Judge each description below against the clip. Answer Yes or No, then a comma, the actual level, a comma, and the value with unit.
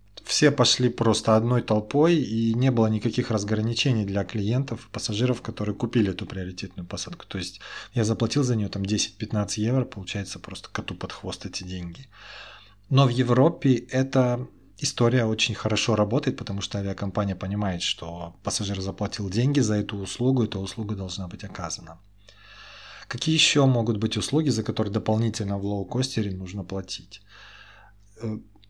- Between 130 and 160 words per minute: Yes, average, 145 wpm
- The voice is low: Yes, low, 110 Hz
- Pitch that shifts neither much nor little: Yes, average, 3.5 semitones